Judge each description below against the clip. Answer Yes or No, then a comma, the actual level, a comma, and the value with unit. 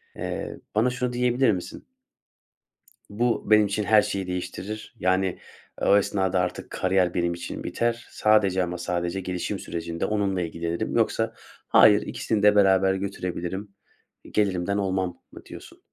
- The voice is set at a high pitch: No, very low, 95 Hz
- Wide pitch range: No, average, 2.8 semitones